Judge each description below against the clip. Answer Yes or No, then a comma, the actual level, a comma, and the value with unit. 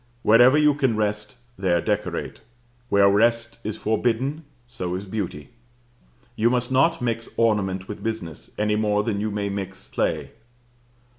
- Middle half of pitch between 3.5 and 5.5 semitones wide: No, average, 2.9 semitones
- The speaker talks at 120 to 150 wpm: Yes, average, 145 wpm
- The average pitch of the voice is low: Yes, low, 110 Hz